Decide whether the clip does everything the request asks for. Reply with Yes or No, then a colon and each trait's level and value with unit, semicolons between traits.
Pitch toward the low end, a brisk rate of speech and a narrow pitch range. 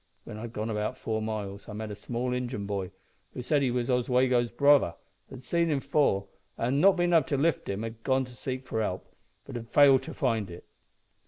No: low, 125 Hz; fast, 220 wpm; average, 3.8 semitones